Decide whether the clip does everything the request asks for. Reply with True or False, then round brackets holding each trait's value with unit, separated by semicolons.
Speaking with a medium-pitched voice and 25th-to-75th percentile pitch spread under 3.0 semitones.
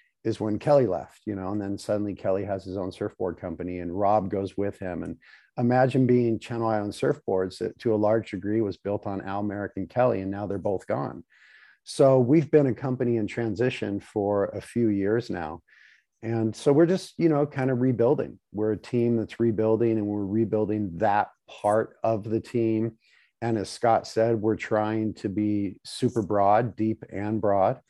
False (110 Hz; 2.6 semitones)